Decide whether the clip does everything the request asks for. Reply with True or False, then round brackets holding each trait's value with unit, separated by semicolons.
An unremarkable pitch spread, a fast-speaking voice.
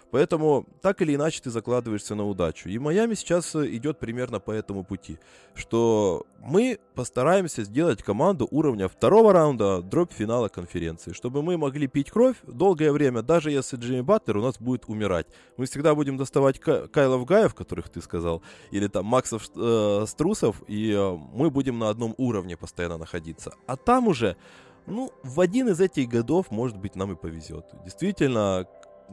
False (7.5 semitones; 165 wpm)